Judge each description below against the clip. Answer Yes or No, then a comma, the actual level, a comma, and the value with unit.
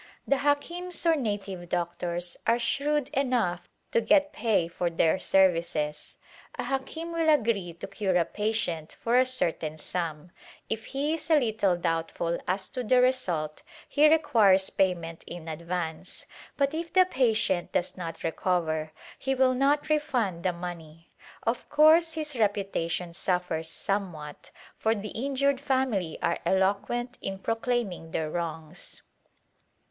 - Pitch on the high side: Yes, high, 200 Hz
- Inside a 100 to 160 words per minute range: Yes, average, 145 wpm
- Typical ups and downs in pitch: No, wide, 7.5 semitones